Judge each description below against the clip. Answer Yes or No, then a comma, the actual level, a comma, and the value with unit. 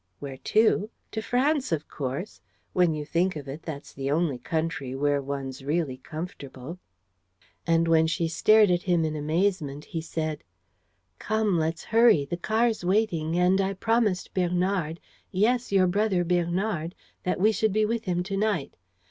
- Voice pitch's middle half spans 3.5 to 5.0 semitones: Yes, average, 4.6 semitones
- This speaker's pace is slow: No, average, 160 wpm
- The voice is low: No, medium, 175 Hz